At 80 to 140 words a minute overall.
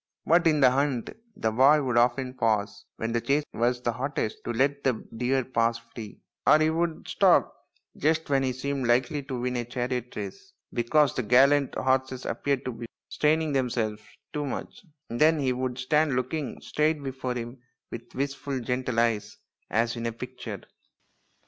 No: average, 175 wpm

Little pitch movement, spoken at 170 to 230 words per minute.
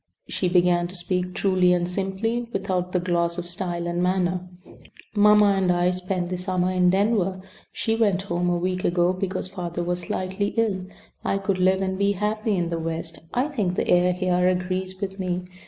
Yes: narrow, 1.4 semitones; average, 190 wpm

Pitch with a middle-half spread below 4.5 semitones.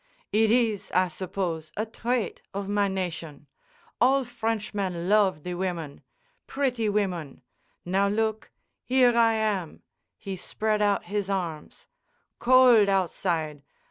Yes: average, 3.7 semitones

